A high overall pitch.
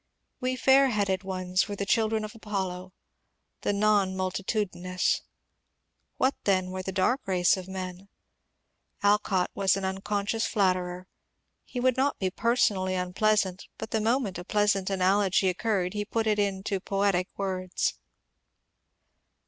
Yes: high, 195 Hz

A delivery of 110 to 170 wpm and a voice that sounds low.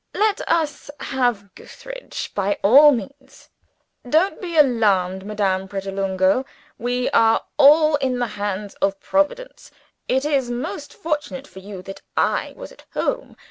No: average, 140 wpm; high, 245 Hz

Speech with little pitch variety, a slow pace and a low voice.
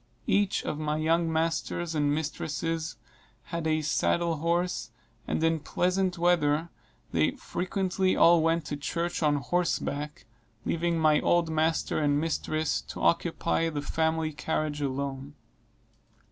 No: narrow, 2.1 semitones; slow, 130 wpm; medium, 160 Hz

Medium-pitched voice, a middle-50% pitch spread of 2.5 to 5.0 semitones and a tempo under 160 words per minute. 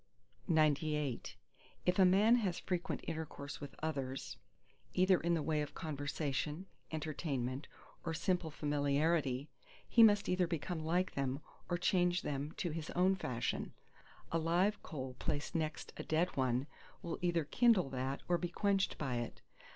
Yes: medium, 160 Hz; average, 4.0 semitones; average, 150 wpm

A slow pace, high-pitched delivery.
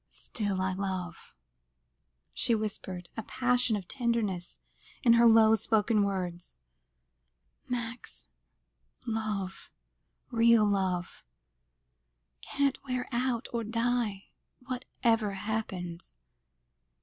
Yes: slow, 90 wpm; high, 220 Hz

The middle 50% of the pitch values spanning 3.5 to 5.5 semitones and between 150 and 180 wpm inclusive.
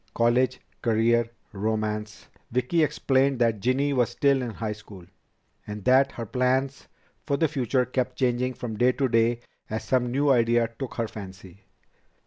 No: average, 2.8 semitones; average, 155 wpm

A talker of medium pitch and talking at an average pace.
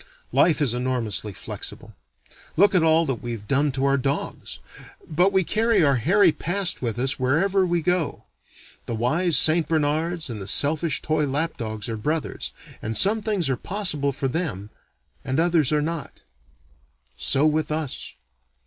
Yes: medium, 150 Hz; average, 160 wpm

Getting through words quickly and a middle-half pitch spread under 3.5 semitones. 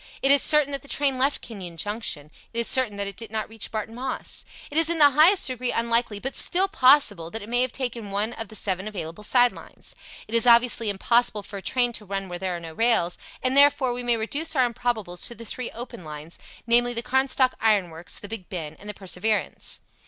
No: fast, 235 wpm; average, 4.2 semitones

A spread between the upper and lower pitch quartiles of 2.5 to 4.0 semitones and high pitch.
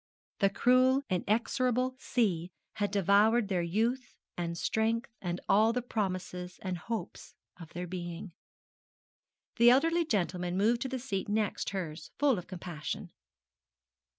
No: average, 5.1 semitones; high, 205 Hz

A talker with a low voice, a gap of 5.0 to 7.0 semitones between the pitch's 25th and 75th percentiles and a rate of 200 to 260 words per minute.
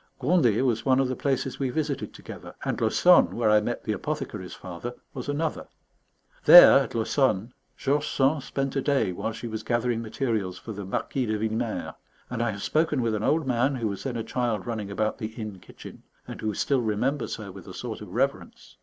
No: low, 120 Hz; average, 4.0 semitones; fast, 205 wpm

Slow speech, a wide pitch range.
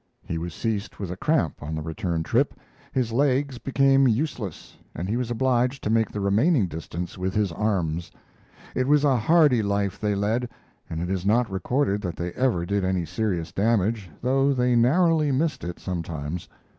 No: average, 180 wpm; wide, 6.2 semitones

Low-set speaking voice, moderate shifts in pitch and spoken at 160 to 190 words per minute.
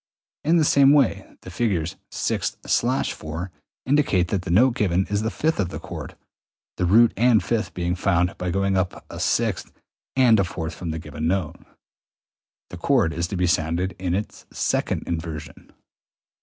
Yes: very low, 95 Hz; average, 4.6 semitones; average, 170 wpm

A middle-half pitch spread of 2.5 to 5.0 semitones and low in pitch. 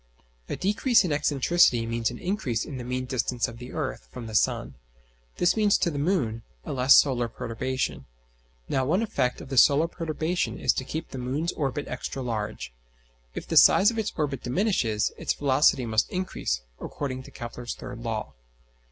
No: wide, 5.5 semitones; low, 130 Hz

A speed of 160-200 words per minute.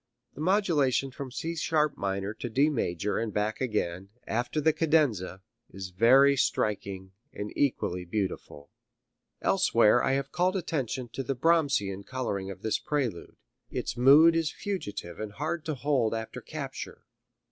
No: average, 145 wpm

